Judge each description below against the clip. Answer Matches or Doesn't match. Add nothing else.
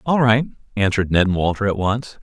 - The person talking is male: Matches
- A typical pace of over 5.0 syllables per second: Matches